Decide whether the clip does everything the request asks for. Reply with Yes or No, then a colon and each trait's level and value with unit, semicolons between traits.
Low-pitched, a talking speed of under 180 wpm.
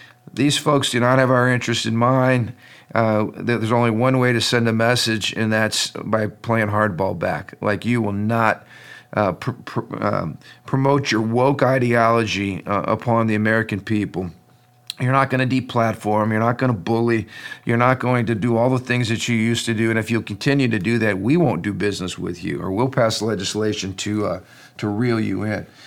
No: low, 115 Hz; fast, 205 wpm